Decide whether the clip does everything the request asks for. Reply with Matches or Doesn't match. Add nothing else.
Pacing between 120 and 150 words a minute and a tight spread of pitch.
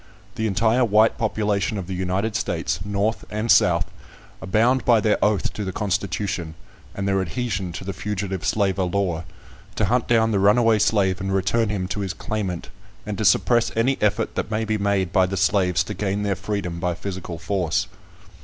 Doesn't match